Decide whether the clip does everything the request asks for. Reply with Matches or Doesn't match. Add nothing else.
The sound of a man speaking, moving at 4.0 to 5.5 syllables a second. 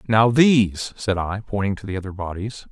Matches